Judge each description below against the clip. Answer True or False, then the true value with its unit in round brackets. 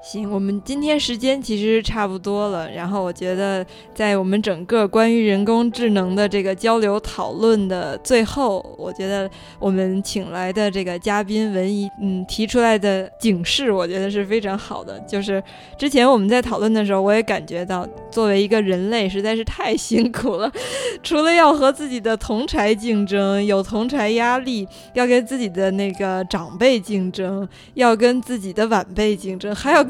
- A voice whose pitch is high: True (210 Hz)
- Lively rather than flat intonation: False (3.0 semitones)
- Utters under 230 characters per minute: False (275 characters per minute)